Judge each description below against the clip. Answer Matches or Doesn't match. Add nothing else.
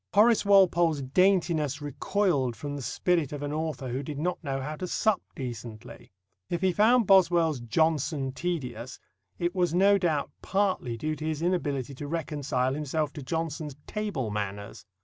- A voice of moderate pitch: Matches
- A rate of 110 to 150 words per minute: Doesn't match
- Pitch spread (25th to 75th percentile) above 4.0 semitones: Matches